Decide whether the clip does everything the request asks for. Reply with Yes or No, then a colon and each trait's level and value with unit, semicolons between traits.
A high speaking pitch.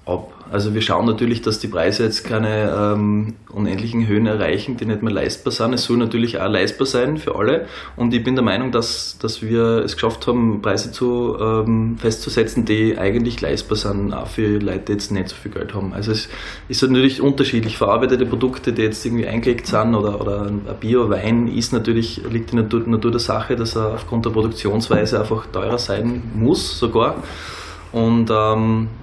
No: low, 110 Hz